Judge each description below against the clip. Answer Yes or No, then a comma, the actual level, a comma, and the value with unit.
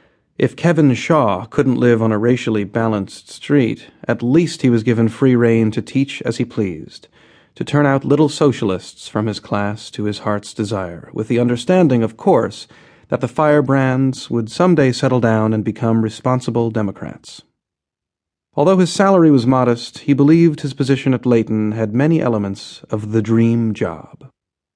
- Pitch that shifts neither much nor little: Yes, average, 4.4 semitones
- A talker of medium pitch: No, low, 120 Hz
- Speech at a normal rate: Yes, average, 165 wpm